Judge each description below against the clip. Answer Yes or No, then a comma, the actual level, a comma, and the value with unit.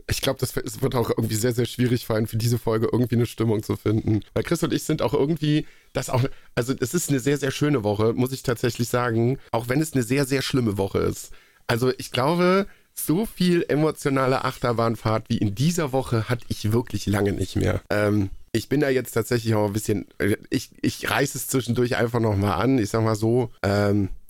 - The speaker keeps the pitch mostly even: No, average, 3.4 semitones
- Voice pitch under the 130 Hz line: Yes, low, 120 Hz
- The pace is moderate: No, fast, 215 wpm